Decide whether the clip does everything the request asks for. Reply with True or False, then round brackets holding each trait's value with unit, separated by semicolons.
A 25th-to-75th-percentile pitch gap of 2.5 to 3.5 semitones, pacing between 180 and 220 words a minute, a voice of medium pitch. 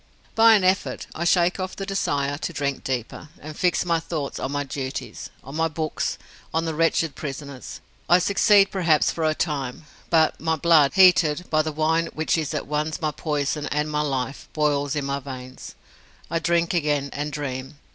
True (2.8 semitones; 185 wpm; 155 Hz)